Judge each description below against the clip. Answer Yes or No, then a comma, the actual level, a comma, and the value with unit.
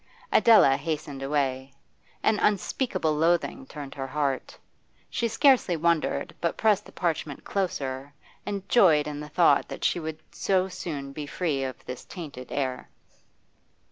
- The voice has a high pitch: No, medium, 155 Hz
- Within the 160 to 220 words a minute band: No, average, 140 wpm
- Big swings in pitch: No, average, 5.0 semitones